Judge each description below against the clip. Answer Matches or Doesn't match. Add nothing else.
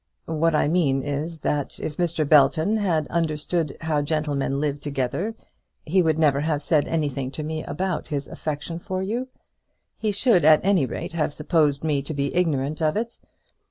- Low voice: Doesn't match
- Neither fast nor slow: Matches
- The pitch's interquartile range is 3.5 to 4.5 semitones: Doesn't match